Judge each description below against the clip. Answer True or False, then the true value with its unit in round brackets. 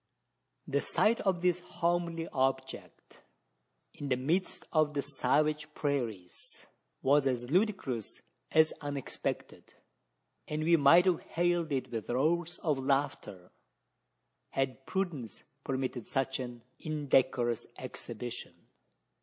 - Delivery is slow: True (110 wpm)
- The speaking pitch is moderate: True (145 Hz)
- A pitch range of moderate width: True (4.3 semitones)